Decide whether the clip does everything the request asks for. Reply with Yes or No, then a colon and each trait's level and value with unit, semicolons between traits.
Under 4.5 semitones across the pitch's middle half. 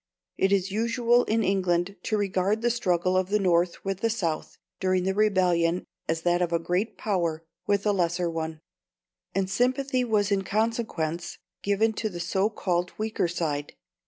Yes: average, 3.6 semitones